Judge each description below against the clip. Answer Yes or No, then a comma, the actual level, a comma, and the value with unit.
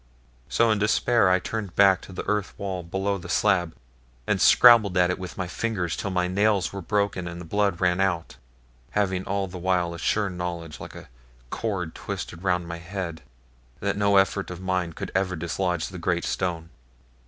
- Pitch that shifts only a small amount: Yes, narrow, 2.3 semitones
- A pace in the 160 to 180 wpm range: No, average, 190 wpm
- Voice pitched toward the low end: Yes, very low, 95 Hz